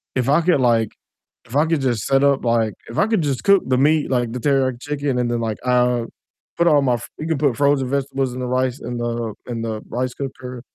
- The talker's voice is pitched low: Yes, low, 130 Hz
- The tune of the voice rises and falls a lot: No, average, 2.9 semitones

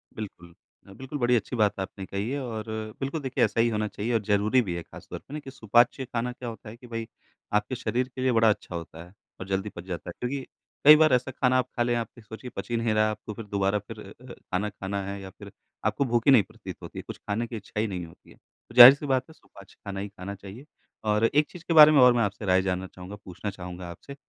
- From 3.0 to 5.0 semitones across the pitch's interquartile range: Yes, average, 4.1 semitones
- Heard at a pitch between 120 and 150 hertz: No, low, 110 Hz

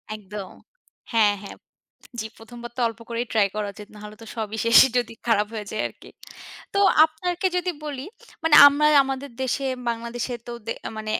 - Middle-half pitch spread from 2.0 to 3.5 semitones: No, average, 3.9 semitones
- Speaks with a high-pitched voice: Yes, high, 230 Hz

